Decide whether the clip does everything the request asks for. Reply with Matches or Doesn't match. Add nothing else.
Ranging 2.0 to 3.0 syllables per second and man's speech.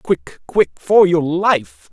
Matches